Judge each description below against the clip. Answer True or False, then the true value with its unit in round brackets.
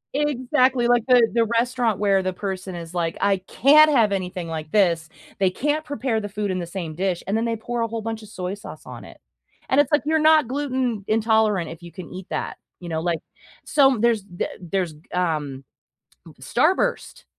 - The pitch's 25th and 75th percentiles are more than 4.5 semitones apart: True (5.2 semitones)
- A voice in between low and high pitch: False (210 Hz)